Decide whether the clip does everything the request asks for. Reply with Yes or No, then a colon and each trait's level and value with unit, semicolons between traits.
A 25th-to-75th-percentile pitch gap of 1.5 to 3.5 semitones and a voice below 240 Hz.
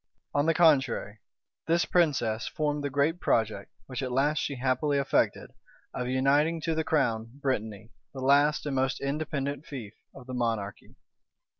Yes: average, 3.2 semitones; low, 135 Hz